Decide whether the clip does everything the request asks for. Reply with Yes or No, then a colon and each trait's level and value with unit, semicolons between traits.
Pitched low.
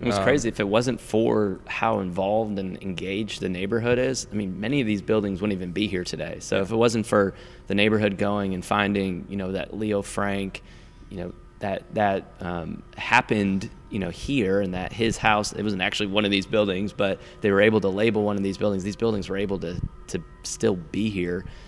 Yes: low, 100 Hz